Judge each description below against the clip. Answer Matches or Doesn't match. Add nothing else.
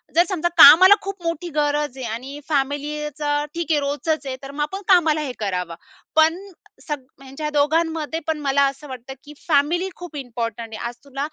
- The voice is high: Matches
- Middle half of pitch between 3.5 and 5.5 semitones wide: Doesn't match